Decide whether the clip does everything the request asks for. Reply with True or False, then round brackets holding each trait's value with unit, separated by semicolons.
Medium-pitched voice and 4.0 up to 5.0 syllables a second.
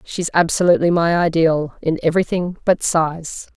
True (165 Hz; 4.9 syllables/s)